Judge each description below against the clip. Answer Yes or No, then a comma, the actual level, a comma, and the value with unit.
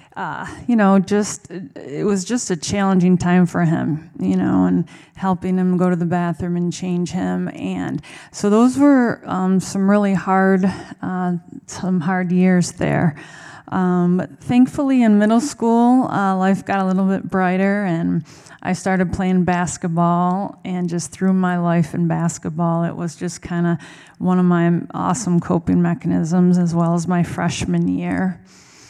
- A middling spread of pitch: No, narrow, 2.0 semitones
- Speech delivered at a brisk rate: No, average, 165 wpm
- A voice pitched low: No, medium, 180 Hz